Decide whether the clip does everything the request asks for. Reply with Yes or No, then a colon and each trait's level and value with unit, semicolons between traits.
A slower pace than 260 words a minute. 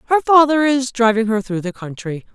Yes: fast, 205 wpm